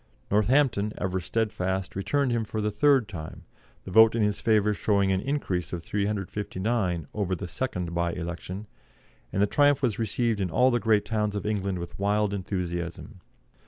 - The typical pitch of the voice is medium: No, low, 105 Hz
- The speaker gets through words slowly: No, average, 170 wpm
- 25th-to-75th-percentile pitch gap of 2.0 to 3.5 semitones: Yes, average, 3.2 semitones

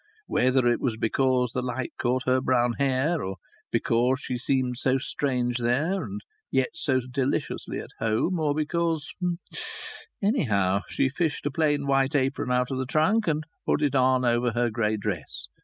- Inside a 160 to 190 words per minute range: Yes, average, 170 wpm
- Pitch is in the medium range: No, low, 130 Hz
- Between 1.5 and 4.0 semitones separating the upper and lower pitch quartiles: Yes, average, 3.1 semitones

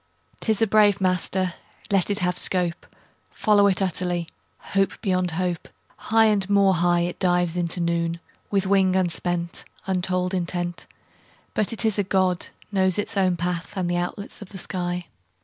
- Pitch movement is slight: Yes, narrow, 1.9 semitones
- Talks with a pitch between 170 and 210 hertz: Yes, medium, 185 Hz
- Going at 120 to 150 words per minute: No, average, 165 wpm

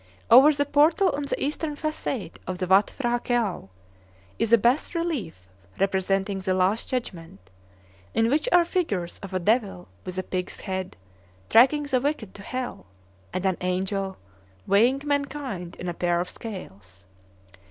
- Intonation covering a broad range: Yes, wide, 7.2 semitones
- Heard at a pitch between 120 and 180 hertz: No, high, 205 Hz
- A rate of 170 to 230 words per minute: No, average, 155 wpm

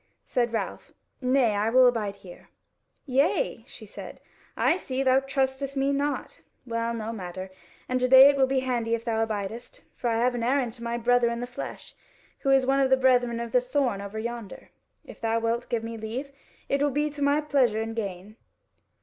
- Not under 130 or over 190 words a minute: No, fast, 205 wpm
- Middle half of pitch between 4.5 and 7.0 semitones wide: No, average, 2.9 semitones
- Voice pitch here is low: No, high, 245 Hz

